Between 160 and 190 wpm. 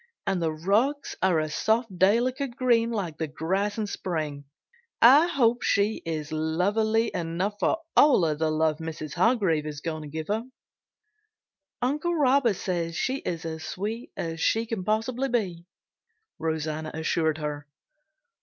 No: average, 145 wpm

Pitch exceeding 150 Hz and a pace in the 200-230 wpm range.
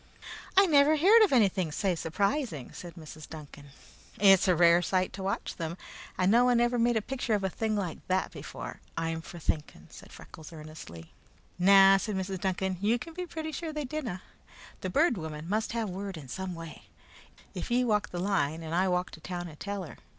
Yes: high, 190 Hz; fast, 205 wpm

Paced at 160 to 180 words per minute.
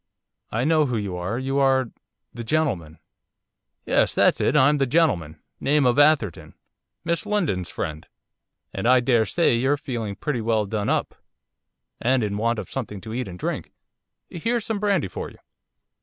Yes: average, 165 wpm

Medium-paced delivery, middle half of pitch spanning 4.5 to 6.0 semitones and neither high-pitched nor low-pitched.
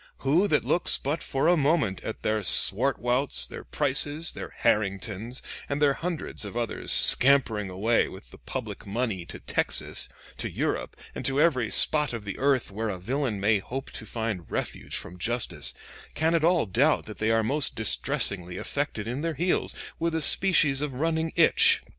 No: average, 175 wpm; wide, 5.6 semitones; low, 125 Hz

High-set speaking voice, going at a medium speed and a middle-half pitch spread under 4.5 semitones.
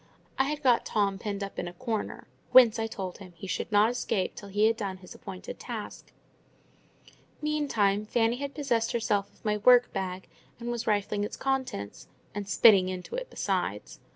Yes: high, 210 Hz; average, 180 wpm; average, 3.6 semitones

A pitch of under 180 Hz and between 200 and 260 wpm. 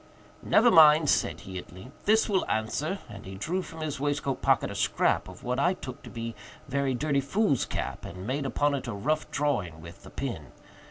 Yes: medium, 140 Hz; fast, 205 wpm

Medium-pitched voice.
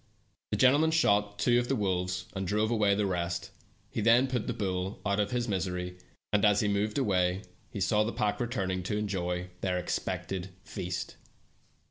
No: low, 100 Hz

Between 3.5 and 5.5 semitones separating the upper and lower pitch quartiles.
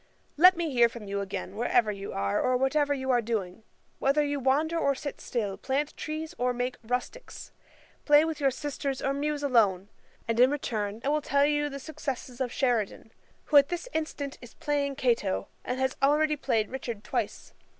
Yes: average, 3.8 semitones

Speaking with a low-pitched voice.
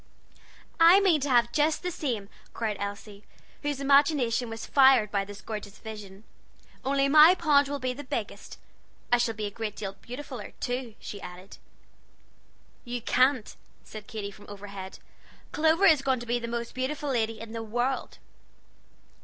No: high, 240 Hz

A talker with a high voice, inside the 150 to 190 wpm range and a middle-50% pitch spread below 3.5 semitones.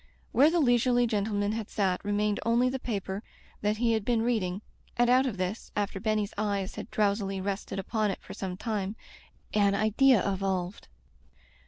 Yes: high, 210 Hz; average, 170 wpm; average, 2.8 semitones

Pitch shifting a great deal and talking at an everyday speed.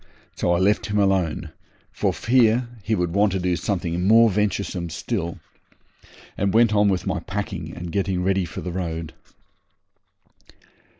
No: average, 3.0 semitones; average, 155 wpm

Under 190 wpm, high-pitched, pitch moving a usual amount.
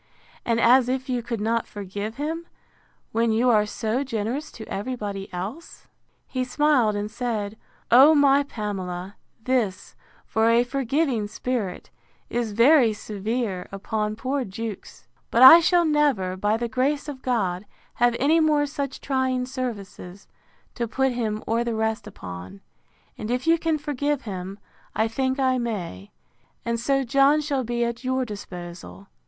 Yes: average, 155 wpm; high, 235 Hz; average, 4.2 semitones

